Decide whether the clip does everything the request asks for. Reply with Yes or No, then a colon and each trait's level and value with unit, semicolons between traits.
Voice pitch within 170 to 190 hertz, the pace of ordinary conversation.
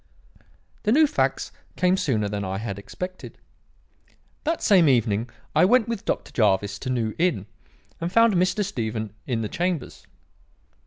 No: low, 135 Hz; average, 150 wpm